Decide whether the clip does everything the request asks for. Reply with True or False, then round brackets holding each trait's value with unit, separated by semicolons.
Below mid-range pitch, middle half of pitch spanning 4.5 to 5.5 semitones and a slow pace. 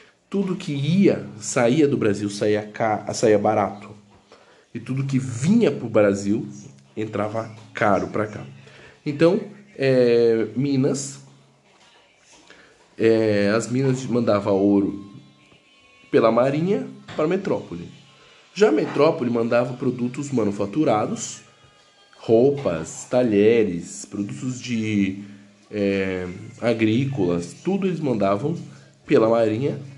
True (115 Hz; 5.1 semitones; 100 wpm)